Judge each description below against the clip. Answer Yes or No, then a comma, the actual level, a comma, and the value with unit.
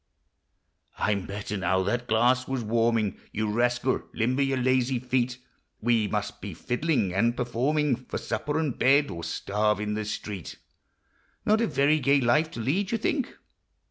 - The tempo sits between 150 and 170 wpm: Yes, average, 160 wpm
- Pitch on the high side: No, low, 120 Hz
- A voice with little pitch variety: No, average, 4.2 semitones